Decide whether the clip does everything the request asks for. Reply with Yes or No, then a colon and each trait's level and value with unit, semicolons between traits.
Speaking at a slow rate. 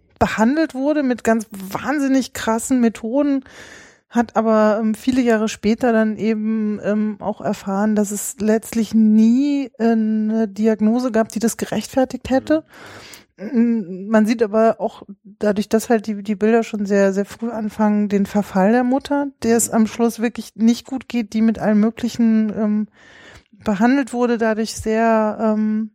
No: average, 155 wpm